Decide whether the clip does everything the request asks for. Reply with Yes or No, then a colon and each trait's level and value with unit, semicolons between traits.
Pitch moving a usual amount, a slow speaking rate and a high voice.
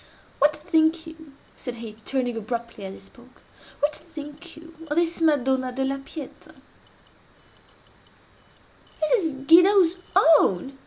Yes: average, 4.0 semitones; slow, 115 wpm; very high, 295 Hz